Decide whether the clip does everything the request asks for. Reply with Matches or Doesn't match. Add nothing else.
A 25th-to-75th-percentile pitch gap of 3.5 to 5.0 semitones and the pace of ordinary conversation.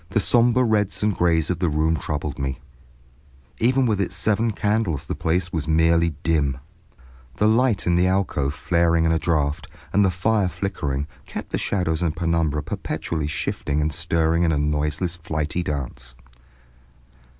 Matches